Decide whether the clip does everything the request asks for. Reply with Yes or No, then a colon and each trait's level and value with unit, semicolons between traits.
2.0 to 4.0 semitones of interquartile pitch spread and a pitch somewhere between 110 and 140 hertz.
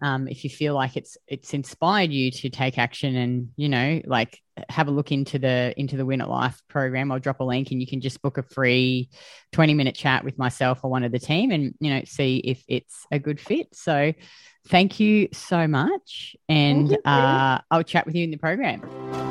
Yes: average, 2.8 semitones; low, 135 Hz